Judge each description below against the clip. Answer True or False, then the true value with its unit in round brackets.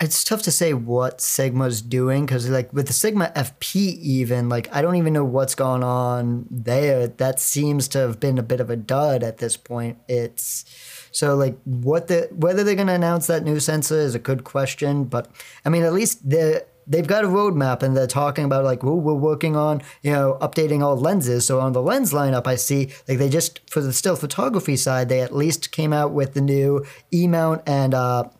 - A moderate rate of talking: False (220 wpm)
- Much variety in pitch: False (3.6 semitones)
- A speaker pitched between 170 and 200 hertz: False (140 Hz)